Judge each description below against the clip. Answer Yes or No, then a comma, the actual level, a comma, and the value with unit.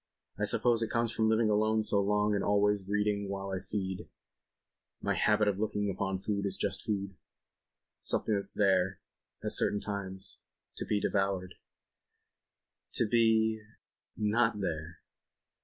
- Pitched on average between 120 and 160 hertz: No, low, 105 Hz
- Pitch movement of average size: No, narrow, 1.8 semitones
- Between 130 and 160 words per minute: Yes, average, 140 wpm